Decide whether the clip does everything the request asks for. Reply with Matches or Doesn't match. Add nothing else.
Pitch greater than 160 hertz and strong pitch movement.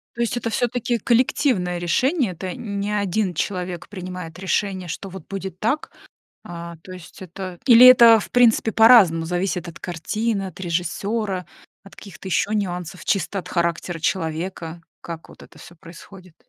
Doesn't match